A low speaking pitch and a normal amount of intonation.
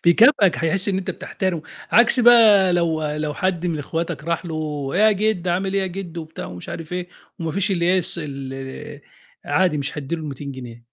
No: medium, 170 Hz; average, 4.0 semitones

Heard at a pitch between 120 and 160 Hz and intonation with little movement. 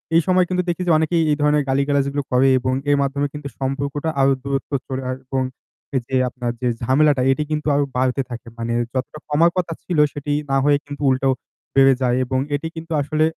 Yes: medium, 140 Hz; narrow, 2.3 semitones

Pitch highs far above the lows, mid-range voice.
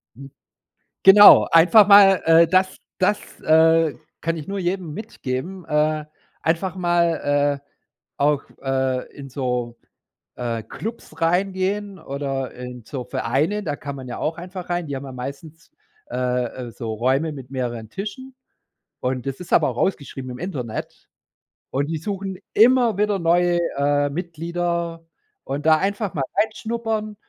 Yes: wide, 5.7 semitones; medium, 160 Hz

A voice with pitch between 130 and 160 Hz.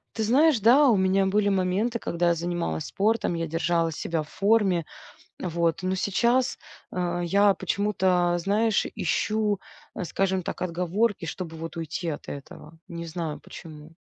No: medium, 185 Hz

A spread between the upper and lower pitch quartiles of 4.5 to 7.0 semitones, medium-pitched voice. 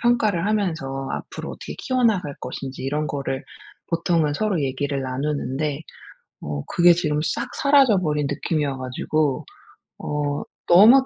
Yes: average, 5.1 semitones; medium, 150 Hz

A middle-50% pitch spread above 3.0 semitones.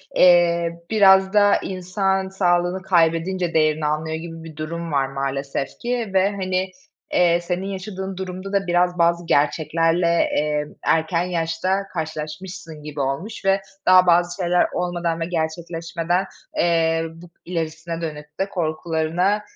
No: narrow, 2.5 semitones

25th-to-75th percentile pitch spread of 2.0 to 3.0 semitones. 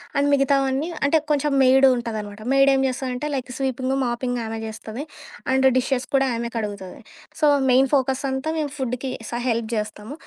Yes: average, 2.7 semitones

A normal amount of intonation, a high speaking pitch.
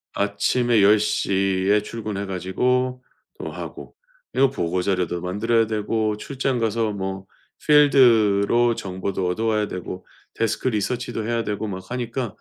No: average, 3.4 semitones; low, 105 Hz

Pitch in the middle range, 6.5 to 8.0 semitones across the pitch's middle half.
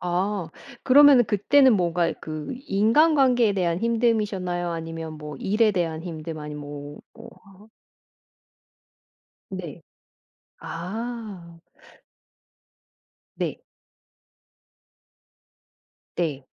No: medium, 180 Hz; average, 5.3 semitones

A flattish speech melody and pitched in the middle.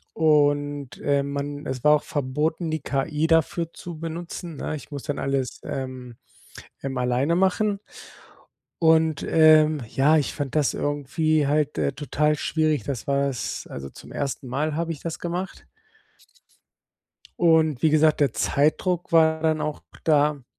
Yes: narrow, 2.3 semitones; medium, 150 Hz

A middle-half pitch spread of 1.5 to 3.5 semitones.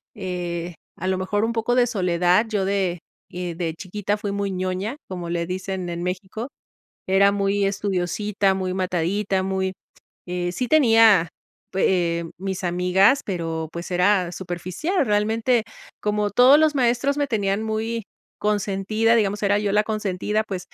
Yes: average, 2.9 semitones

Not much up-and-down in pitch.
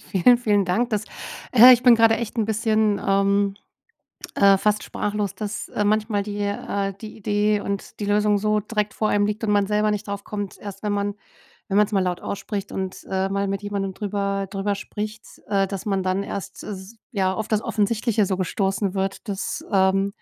Yes: narrow, 1.4 semitones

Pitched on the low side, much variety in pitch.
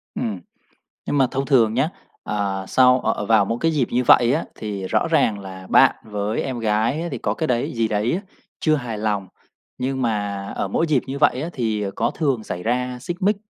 No: low, 115 Hz; average, 4.2 semitones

